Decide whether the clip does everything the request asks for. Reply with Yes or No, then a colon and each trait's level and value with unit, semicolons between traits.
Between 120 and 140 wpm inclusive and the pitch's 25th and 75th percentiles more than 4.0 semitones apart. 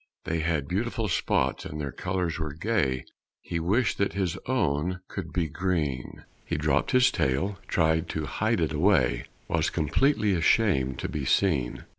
No: average, 160 wpm; average, 4.8 semitones